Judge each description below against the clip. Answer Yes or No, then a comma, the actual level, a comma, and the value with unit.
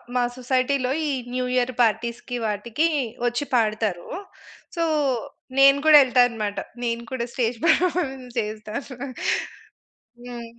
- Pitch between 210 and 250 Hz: Yes, high, 245 Hz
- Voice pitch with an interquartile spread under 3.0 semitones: Yes, narrow, 2.5 semitones